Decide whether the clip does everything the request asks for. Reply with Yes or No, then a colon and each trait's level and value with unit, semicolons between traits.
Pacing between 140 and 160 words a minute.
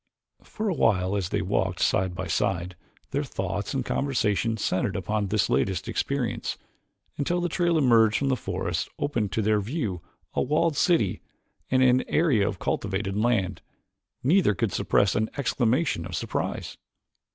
Yes: average, 155 wpm